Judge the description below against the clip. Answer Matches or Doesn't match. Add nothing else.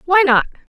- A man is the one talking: Doesn't match